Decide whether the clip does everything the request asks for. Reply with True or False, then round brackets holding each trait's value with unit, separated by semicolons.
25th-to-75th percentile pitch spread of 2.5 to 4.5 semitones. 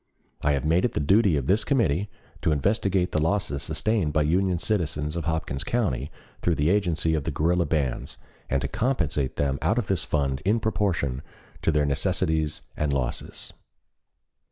False (5.1 semitones)